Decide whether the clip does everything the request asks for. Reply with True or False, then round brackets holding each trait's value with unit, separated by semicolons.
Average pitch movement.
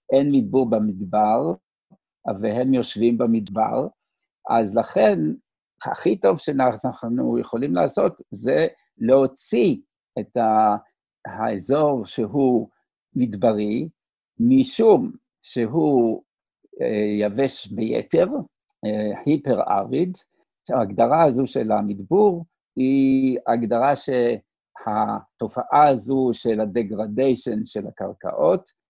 True (4.0 semitones)